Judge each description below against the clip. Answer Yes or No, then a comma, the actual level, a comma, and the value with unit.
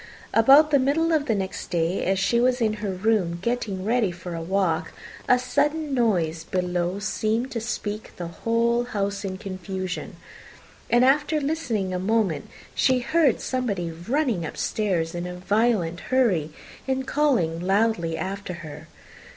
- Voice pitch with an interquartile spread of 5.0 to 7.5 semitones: Yes, wide, 5.6 semitones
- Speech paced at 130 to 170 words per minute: Yes, average, 150 wpm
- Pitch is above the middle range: Yes, high, 205 Hz